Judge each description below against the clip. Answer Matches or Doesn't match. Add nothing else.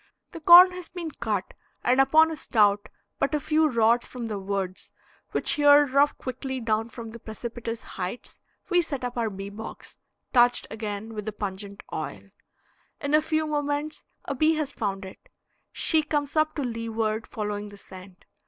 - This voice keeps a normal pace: Matches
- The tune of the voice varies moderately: Doesn't match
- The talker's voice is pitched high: Matches